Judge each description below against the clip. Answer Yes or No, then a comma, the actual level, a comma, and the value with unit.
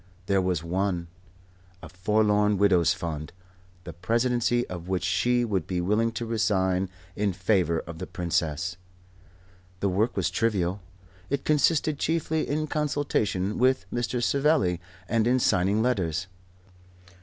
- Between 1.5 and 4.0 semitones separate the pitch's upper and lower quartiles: No, average, 5.0 semitones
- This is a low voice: Yes, low, 100 Hz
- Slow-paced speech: Yes, slow, 130 wpm